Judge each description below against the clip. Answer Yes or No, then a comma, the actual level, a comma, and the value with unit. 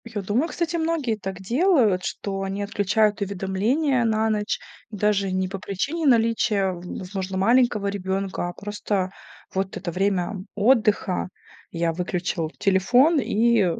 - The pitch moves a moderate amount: Yes, average, 3.4 semitones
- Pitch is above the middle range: Yes, high, 205 Hz